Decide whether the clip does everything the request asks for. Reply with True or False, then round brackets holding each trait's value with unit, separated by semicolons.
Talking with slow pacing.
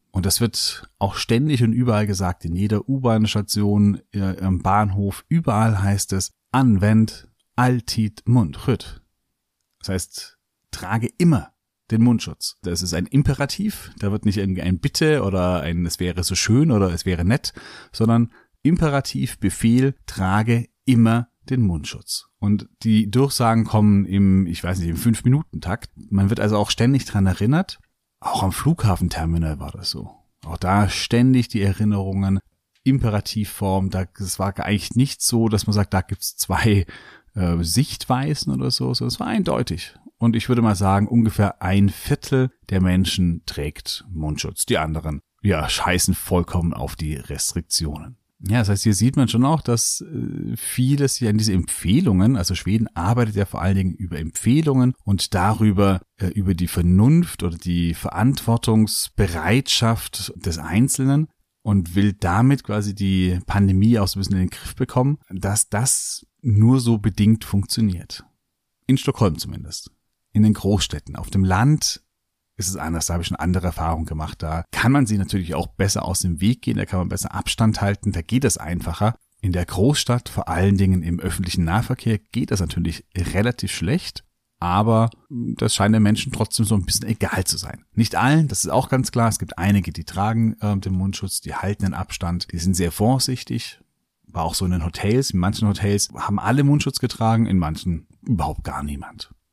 False (170 wpm)